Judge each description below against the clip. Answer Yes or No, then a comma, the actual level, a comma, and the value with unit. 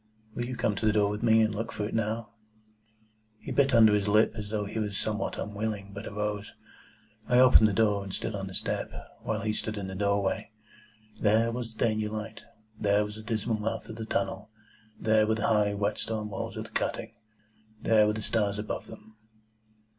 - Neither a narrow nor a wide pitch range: No, narrow, 1.3 semitones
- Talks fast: Yes, fast, 210 wpm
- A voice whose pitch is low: Yes, low, 105 Hz